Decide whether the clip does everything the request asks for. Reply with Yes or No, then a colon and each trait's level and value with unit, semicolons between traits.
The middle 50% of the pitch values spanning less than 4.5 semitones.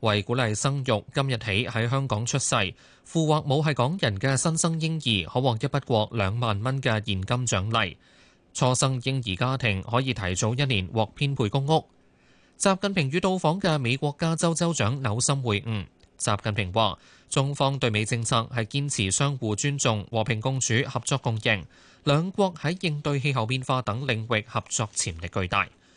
No: average, 4.8 semitones